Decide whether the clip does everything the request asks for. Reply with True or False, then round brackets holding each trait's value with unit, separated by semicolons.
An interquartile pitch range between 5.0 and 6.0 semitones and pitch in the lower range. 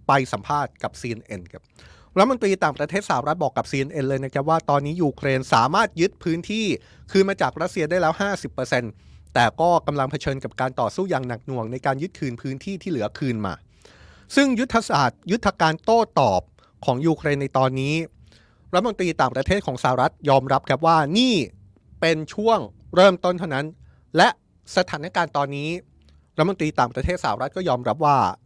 False (5.6 semitones; 145 Hz)